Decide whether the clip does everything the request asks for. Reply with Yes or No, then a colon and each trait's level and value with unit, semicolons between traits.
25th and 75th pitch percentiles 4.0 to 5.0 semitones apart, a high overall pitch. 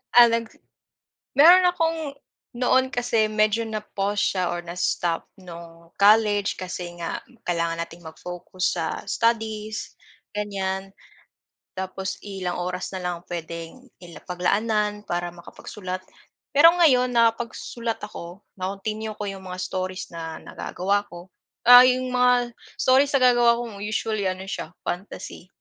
Yes: average, 4.5 semitones; high, 205 Hz